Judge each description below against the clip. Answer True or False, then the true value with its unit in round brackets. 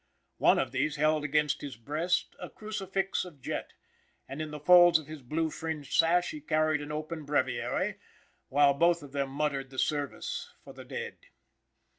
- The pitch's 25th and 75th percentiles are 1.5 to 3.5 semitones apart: True (2.8 semitones)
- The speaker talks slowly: False (175 wpm)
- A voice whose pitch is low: False (150 Hz)